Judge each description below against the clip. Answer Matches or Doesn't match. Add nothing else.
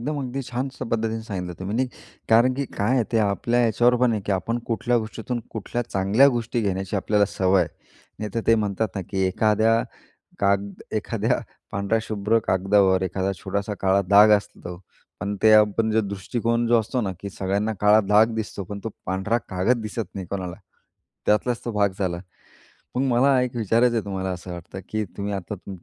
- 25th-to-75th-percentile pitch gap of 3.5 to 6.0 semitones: Doesn't match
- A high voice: Doesn't match